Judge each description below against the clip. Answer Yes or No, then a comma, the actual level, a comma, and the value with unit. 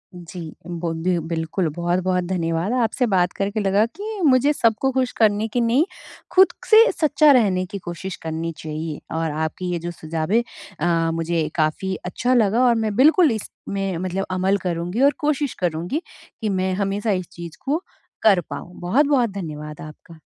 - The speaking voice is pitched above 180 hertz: Yes, high, 190 Hz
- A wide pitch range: Yes, wide, 6.0 semitones